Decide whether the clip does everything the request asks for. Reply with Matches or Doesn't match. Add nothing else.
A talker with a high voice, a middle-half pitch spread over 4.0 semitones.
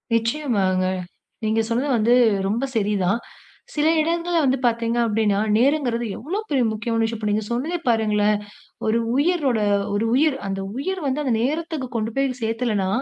Matches